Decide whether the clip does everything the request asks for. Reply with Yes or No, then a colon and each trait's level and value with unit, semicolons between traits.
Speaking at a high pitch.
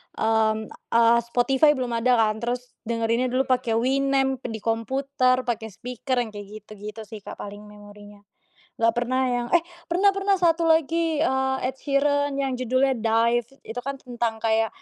Yes: high, 245 Hz